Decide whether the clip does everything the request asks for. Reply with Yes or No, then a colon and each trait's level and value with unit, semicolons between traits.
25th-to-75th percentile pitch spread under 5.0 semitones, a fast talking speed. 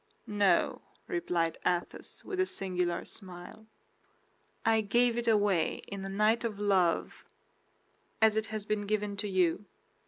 No: average, 2.9 semitones; slow, 135 wpm